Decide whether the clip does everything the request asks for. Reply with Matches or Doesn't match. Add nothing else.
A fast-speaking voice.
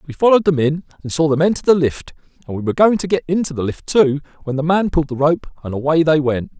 Matches